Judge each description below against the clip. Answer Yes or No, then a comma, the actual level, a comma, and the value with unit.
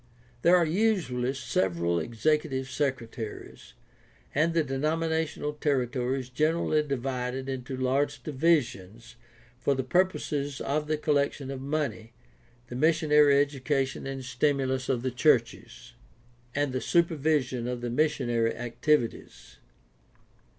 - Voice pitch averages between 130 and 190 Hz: Yes, low, 135 Hz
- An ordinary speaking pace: No, slow, 120 wpm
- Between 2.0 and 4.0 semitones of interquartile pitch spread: Yes, average, 3.4 semitones